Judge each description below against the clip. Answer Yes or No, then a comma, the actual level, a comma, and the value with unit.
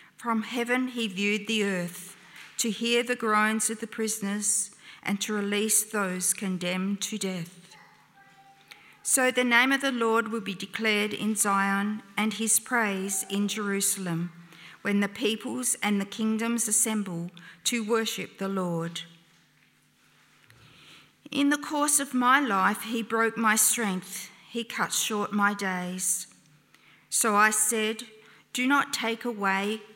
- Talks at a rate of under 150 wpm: Yes, average, 140 wpm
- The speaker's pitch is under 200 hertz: No, high, 210 Hz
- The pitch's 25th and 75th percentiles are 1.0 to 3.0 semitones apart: Yes, average, 2.7 semitones